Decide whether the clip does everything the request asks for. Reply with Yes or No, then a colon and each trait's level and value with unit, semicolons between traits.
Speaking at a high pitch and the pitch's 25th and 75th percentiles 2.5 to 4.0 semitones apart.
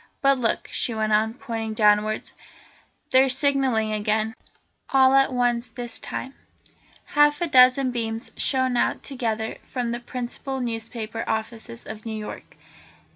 Yes: high, 235 Hz; average, 2.9 semitones